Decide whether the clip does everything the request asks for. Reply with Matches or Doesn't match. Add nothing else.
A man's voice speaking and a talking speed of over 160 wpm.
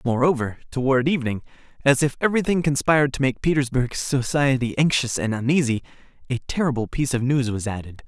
Doesn't match